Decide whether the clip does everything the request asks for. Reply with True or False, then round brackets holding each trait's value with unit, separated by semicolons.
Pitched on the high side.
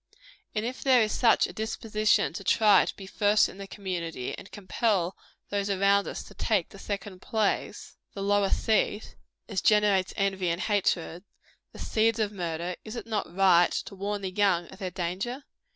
True (200 Hz)